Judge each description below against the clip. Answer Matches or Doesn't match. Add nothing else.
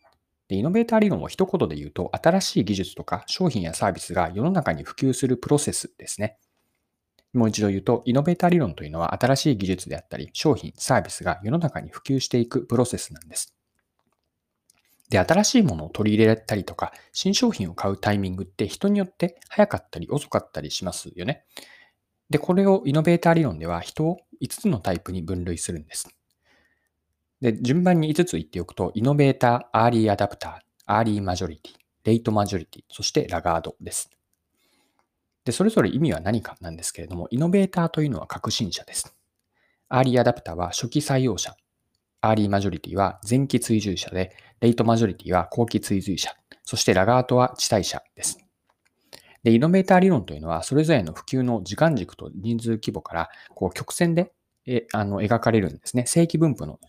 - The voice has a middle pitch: Doesn't match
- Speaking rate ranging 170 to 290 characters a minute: Doesn't match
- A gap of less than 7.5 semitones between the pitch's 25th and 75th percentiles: Doesn't match